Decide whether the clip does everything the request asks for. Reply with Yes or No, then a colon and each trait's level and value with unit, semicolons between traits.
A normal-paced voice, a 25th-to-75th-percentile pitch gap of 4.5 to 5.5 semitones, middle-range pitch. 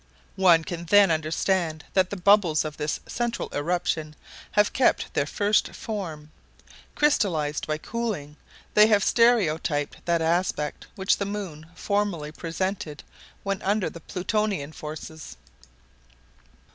No: slow, 120 wpm; average, 4.8 semitones; medium, 175 Hz